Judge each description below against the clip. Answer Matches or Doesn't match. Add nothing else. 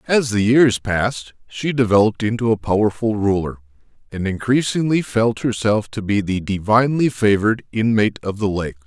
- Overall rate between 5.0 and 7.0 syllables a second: Matches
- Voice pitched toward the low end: Matches